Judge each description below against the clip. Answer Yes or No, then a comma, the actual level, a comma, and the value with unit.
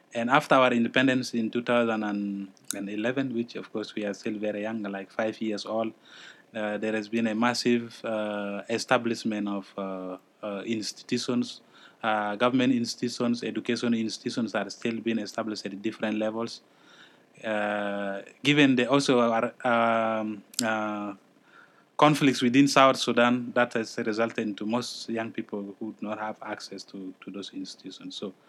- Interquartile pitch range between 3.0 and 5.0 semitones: No, narrow, 2.5 semitones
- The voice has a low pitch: Yes, low, 115 Hz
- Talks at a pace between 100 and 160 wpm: Yes, average, 150 wpm